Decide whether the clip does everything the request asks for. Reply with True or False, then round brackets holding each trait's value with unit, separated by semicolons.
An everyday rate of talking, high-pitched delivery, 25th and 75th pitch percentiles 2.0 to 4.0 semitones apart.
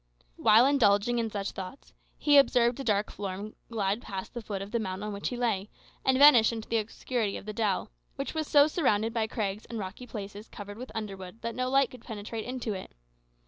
False (215 wpm; 220 Hz; 3.3 semitones)